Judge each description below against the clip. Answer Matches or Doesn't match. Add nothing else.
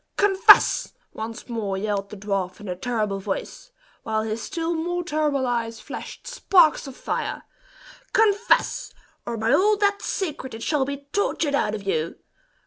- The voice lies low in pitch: Doesn't match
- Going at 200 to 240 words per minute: Doesn't match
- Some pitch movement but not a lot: Doesn't match